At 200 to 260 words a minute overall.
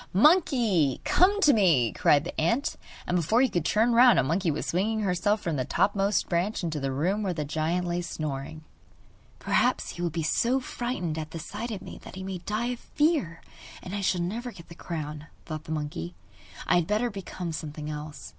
Yes: fast, 205 wpm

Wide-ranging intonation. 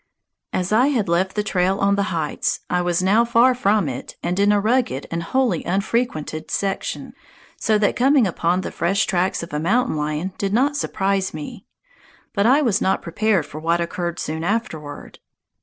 No: average, 4.4 semitones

